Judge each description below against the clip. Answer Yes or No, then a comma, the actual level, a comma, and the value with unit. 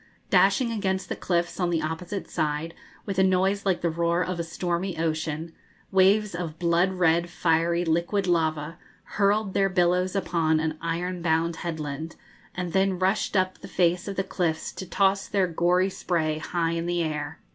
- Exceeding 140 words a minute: Yes, average, 175 wpm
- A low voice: No, medium, 175 Hz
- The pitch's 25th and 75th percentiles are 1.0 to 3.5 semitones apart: Yes, narrow, 2.5 semitones